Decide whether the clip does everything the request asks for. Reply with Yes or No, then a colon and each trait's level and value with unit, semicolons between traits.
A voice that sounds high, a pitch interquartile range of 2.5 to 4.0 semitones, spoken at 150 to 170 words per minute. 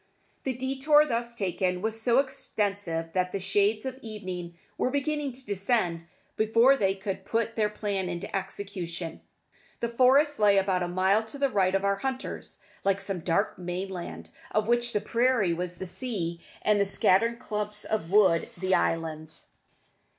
No: high, 200 Hz; average, 4.4 semitones; average, 165 wpm